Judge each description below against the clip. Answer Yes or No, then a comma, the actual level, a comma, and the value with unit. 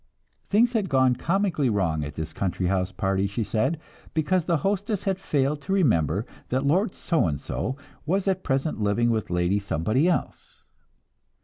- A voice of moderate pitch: No, low, 130 Hz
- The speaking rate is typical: Yes, average, 170 wpm